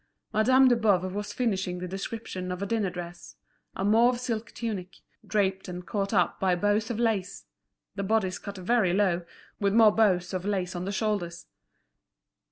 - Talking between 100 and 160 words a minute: No, average, 170 wpm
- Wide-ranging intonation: No, average, 3.2 semitones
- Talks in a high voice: Yes, high, 200 Hz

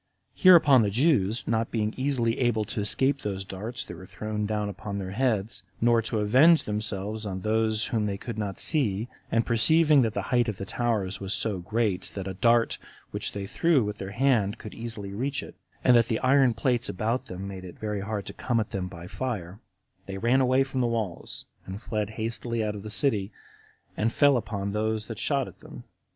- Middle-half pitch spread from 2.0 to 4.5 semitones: Yes, average, 3.1 semitones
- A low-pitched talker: Yes, low, 110 Hz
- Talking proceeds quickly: Yes, fast, 210 wpm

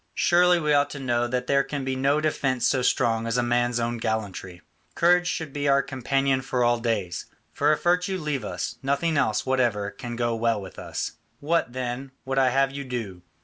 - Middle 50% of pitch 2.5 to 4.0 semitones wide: Yes, average, 3.2 semitones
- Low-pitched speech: Yes, low, 130 Hz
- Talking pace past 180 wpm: Yes, fast, 205 wpm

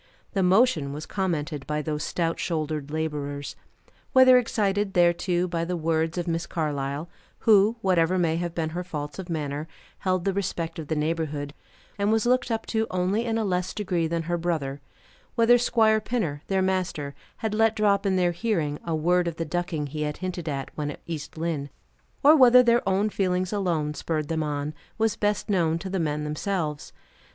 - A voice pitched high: No, medium, 175 Hz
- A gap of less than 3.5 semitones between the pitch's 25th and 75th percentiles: No, average, 4.5 semitones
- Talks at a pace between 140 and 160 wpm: No, average, 190 wpm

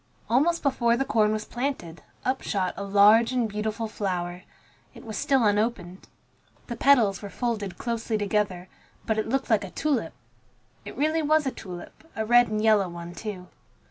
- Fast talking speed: No, average, 175 wpm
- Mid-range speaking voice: No, high, 220 Hz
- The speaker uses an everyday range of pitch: Yes, average, 3.5 semitones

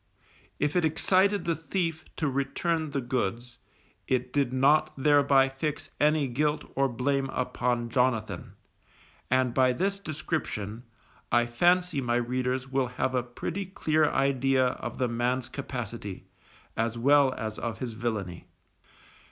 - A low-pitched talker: Yes, low, 130 Hz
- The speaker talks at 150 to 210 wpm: No, slow, 135 wpm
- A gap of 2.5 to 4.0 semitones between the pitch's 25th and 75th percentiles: Yes, average, 3.7 semitones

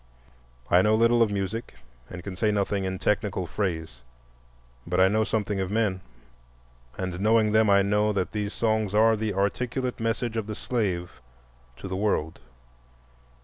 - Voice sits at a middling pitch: No, low, 105 Hz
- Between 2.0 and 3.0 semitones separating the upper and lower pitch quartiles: Yes, average, 2.7 semitones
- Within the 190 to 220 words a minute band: No, average, 160 wpm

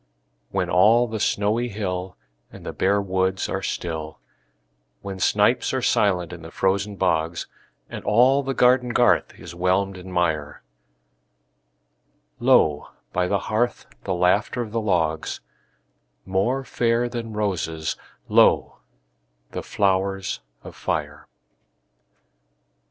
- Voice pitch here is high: No, very low, 95 Hz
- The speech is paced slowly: Yes, slow, 120 wpm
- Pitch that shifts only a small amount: No, average, 3.7 semitones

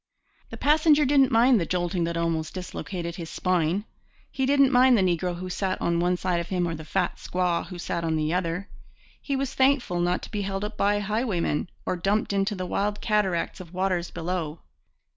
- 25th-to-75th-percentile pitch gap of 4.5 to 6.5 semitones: No, average, 3.5 semitones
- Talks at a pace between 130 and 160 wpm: No, average, 200 wpm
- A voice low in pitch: No, medium, 185 Hz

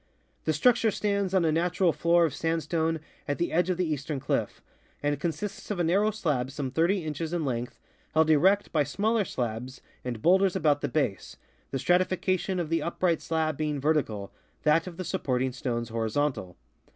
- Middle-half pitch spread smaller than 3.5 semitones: No, average, 4.3 semitones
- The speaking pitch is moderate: Yes, medium, 160 Hz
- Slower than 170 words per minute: No, average, 180 wpm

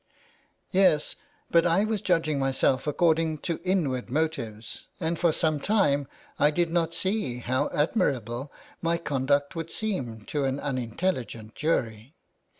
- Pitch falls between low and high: Yes, medium, 150 Hz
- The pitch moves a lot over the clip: No, average, 4.5 semitones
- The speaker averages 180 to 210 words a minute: No, average, 145 wpm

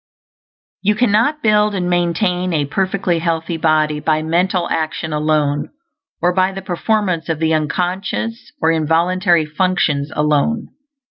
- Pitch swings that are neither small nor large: Yes, average, 3.3 semitones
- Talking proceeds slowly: Yes, slow, 130 wpm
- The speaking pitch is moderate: Yes, medium, 175 Hz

